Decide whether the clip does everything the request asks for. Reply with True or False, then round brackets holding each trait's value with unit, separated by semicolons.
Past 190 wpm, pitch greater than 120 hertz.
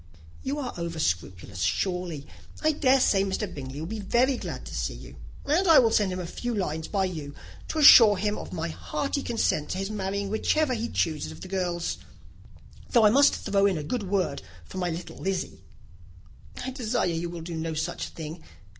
True (200 wpm; 190 Hz)